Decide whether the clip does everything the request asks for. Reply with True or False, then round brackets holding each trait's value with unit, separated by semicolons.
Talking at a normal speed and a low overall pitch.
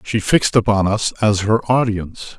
True (175 wpm; 105 Hz)